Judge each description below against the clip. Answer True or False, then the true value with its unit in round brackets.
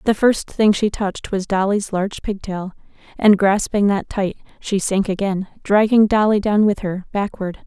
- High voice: True (200 Hz)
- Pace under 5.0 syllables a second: True (4.7 syllables/s)